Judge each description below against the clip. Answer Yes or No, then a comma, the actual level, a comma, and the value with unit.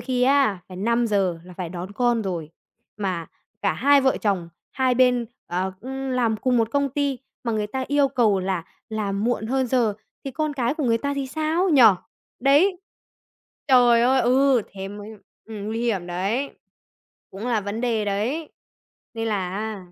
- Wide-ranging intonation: No, average, 4.7 semitones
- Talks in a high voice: Yes, high, 235 Hz